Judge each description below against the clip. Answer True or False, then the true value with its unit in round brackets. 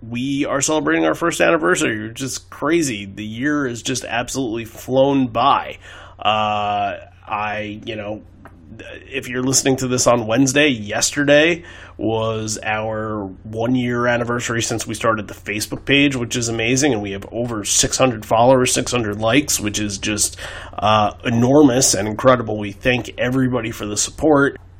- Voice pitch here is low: True (115 Hz)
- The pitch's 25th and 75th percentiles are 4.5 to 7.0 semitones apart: False (3.7 semitones)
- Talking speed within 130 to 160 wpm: True (150 wpm)